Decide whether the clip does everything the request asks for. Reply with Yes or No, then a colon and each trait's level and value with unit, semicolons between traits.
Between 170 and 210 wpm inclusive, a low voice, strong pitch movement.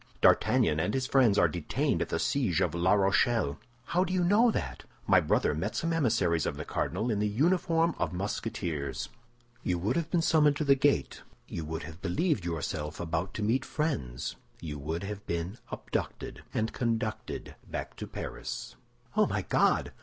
Yes: average, 180 wpm; low, 105 Hz; wide, 9.0 semitones